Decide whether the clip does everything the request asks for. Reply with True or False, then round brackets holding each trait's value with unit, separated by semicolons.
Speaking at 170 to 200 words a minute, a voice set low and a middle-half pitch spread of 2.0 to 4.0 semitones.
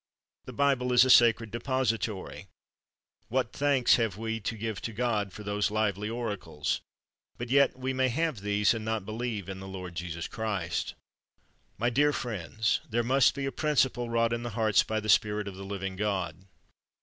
True (180 wpm; 110 Hz; 3.2 semitones)